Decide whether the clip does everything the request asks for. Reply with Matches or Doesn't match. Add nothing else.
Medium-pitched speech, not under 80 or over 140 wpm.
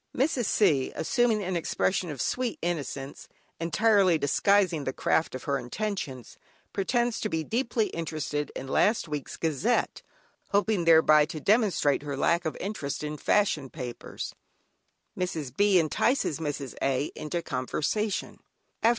Matches